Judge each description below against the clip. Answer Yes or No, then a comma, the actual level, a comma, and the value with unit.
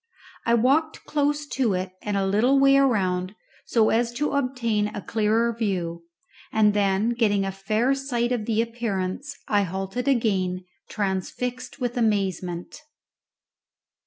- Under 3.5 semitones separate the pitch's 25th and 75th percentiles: No, average, 4.3 semitones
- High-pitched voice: Yes, high, 220 Hz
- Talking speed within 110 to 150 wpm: Yes, slow, 135 wpm